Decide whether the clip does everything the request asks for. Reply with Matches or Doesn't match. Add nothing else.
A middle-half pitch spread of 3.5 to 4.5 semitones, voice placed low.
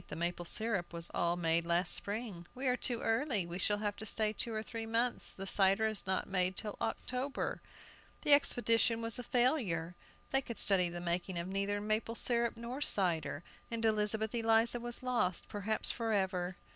Doesn't match